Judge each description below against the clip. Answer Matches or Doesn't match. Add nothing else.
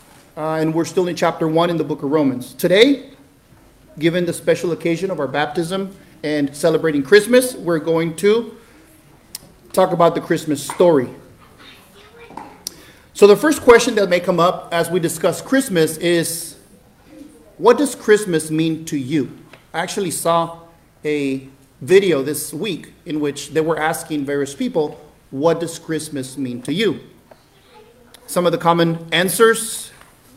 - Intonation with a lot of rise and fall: Doesn't match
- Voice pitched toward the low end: Doesn't match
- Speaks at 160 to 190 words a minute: Doesn't match